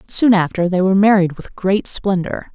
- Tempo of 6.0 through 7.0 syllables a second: No, 5.0 syllables/s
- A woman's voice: Yes, female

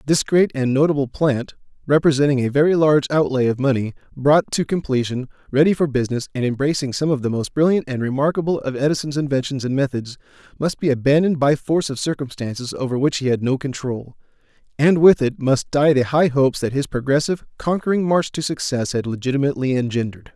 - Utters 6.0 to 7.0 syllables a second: Yes, 6.2 syllables/s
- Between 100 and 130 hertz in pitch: No, medium, 140 Hz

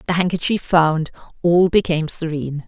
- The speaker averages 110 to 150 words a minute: Yes, slow, 135 wpm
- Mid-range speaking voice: Yes, medium, 165 Hz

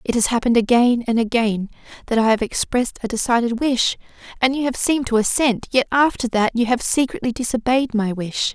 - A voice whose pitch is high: Yes, high, 240 Hz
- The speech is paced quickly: No, average, 195 wpm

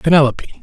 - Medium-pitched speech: Yes, medium, 145 Hz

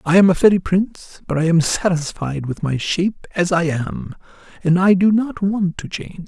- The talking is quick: Yes, fast, 210 wpm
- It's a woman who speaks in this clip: No, male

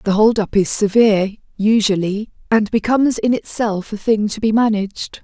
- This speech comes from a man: No, female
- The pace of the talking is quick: No, average, 170 wpm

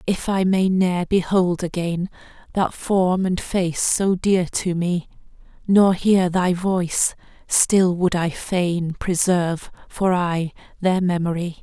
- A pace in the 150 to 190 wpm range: No, average, 140 wpm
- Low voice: No, medium, 180 Hz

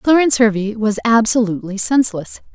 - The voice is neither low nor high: No, high, 225 Hz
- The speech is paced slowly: Yes, slow, 120 wpm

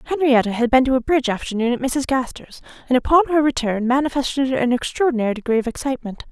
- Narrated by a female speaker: Yes, female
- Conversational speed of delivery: Yes, average, 190 wpm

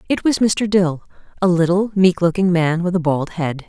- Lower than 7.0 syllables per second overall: Yes, 4.9 syllables/s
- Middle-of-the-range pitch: Yes, medium, 180 Hz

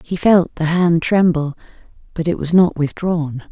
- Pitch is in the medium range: Yes, medium, 165 Hz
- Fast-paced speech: No, average, 170 wpm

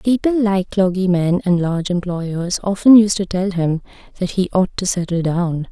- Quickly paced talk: No, average, 180 wpm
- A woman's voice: Yes, female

